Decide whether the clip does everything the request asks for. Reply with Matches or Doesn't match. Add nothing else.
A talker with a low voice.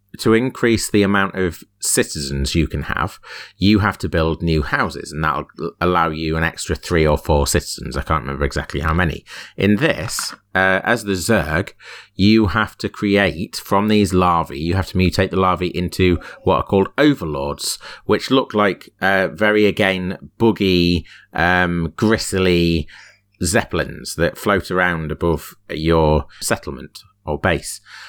Matches